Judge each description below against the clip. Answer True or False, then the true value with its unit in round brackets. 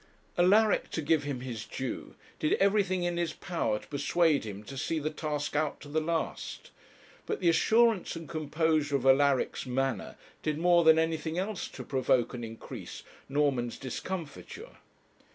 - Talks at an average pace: True (160 wpm)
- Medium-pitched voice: True (155 Hz)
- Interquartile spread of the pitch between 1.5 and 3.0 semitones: False (4.2 semitones)